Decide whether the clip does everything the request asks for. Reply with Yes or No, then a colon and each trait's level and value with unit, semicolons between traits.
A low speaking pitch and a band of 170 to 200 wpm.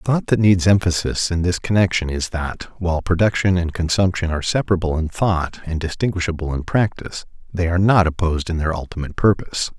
Yes: very low, 90 Hz; average, 185 wpm